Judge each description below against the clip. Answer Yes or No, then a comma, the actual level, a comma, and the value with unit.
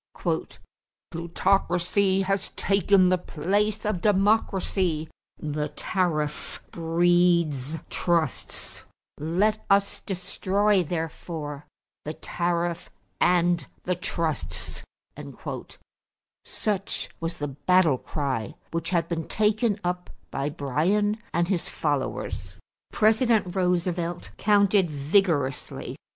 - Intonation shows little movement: No, average, 3.6 semitones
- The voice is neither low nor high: Yes, medium, 175 Hz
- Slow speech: Yes, slow, 90 wpm